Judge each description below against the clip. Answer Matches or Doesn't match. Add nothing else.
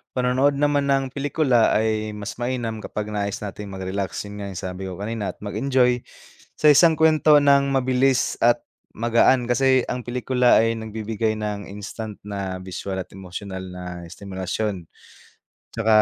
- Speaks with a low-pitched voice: Matches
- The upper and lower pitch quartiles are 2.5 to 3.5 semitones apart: Doesn't match